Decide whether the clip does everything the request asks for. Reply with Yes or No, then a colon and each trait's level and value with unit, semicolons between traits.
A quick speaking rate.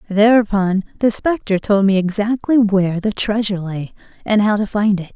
No: average, 175 wpm